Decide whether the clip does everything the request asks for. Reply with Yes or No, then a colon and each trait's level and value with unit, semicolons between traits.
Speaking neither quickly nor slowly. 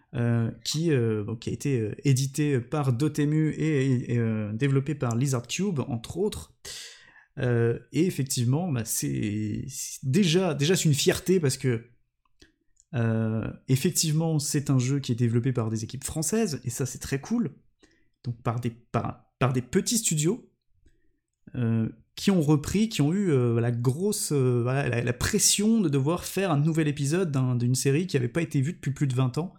Yes: average, 185 wpm